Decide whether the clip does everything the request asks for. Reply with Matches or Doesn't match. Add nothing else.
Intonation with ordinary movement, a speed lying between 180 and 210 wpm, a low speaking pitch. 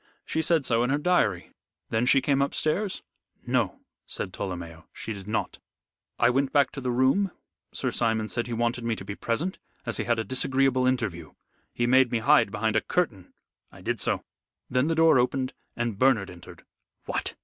Matches